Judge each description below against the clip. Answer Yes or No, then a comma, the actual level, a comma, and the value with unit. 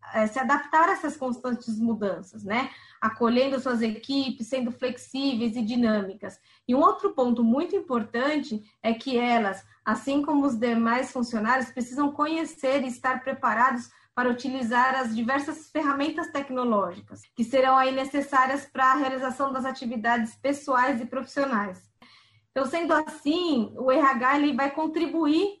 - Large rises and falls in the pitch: No, average, 3.1 semitones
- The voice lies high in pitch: Yes, very high, 260 Hz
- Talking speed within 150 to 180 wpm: No, average, 140 wpm